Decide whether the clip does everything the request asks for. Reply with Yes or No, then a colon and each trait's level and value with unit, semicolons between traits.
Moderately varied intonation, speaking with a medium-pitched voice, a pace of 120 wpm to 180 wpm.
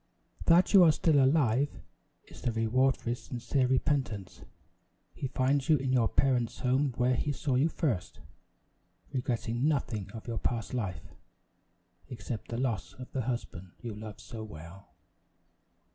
No: average, 3.3 semitones; low, 125 Hz; average, 150 wpm